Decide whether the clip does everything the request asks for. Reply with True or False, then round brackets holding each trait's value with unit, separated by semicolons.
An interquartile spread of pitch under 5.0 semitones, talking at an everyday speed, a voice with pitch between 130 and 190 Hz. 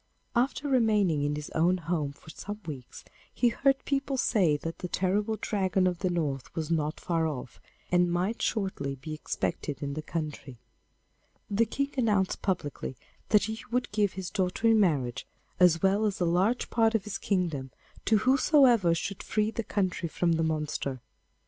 False (5.5 semitones; 175 wpm; 185 Hz)